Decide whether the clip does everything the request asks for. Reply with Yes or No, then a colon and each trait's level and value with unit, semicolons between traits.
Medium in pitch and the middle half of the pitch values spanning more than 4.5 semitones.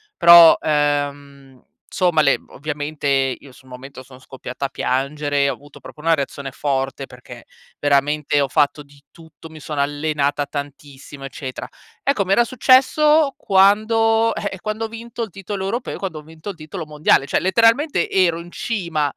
Yes: medium, 150 Hz; wide, 5.6 semitones